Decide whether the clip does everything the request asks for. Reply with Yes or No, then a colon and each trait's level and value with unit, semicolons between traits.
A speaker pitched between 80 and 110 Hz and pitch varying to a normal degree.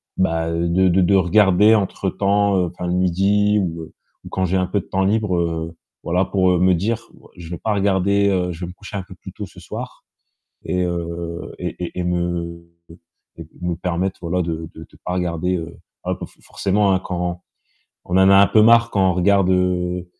No: very low, 90 Hz; narrow, 2.1 semitones